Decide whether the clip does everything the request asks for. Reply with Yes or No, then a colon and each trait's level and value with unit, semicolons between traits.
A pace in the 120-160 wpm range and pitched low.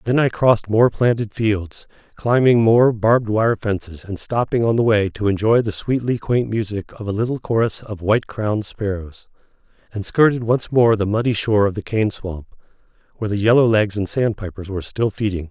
No: average, 180 wpm; low, 110 Hz